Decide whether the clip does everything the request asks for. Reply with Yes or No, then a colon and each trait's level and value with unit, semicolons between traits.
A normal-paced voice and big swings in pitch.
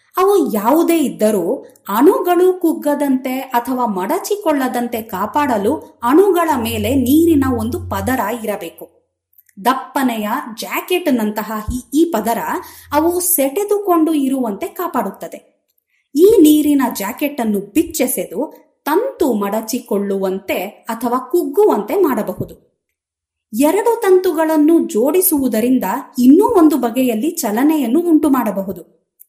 Yes: average, 85 wpm; wide, 6.3 semitones